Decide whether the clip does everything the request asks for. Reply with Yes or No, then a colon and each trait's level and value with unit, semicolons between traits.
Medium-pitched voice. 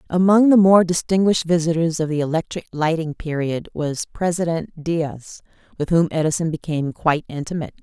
Yes: medium, 165 Hz